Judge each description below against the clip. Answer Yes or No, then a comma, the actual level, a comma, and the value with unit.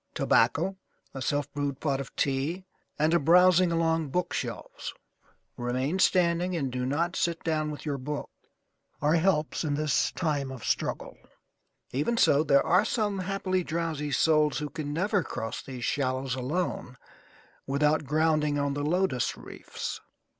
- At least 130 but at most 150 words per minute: Yes, average, 145 wpm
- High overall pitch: No, medium, 150 Hz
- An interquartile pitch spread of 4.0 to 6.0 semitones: No, average, 3.6 semitones